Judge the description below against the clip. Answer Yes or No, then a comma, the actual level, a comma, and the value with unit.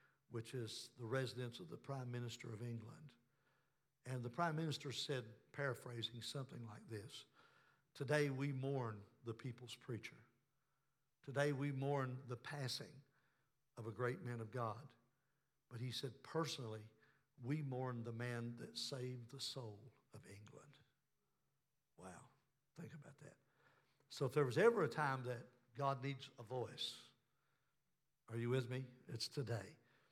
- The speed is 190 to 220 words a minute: No, average, 145 wpm